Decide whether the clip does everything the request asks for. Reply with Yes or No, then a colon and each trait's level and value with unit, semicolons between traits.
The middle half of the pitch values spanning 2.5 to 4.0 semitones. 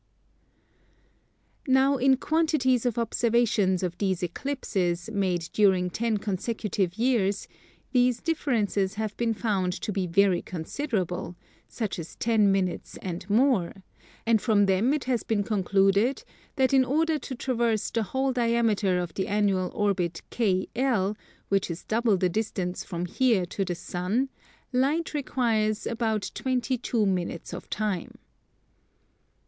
No: average, 4.6 semitones